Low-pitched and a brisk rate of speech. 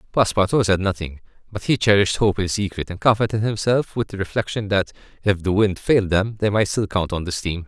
Yes: low, 100 Hz; fast, 220 wpm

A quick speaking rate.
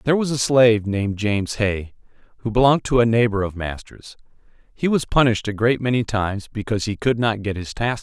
Yes: fast, 215 wpm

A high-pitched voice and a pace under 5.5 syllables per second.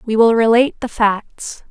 Yes: high, 230 Hz; 4.6 syllables/s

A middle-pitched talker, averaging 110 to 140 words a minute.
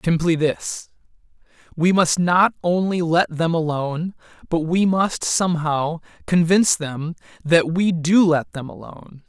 Yes: medium, 170 Hz; slow, 135 wpm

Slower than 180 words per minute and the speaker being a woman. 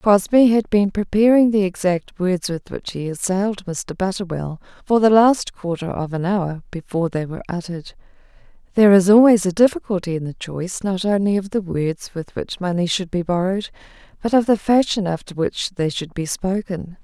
No: average, 185 wpm; female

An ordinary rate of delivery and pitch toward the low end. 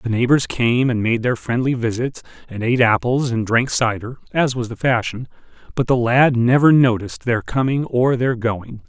Yes: average, 190 wpm; low, 120 Hz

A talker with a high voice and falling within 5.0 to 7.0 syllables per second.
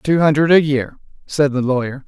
No: medium, 145 Hz; 5.2 syllables/s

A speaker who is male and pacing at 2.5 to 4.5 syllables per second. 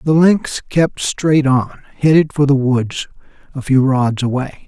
Yes: male; 4.0 syllables/s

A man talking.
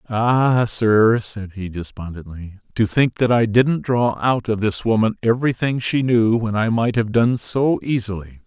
Yes: male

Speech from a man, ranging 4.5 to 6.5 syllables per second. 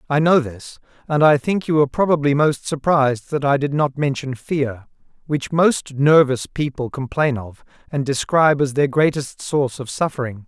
Yes: male; 4.9 syllables/s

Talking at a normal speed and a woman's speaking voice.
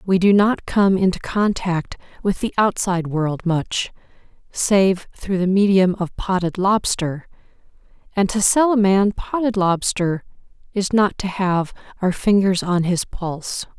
Yes: average, 150 wpm; female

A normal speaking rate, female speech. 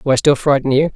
No: fast, 315 wpm; female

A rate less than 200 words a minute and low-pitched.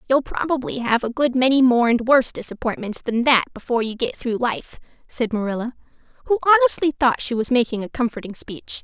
No: average, 190 wpm; high, 245 Hz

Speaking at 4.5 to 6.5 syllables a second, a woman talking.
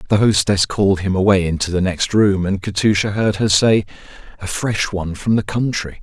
No: 5.3 syllables/s; male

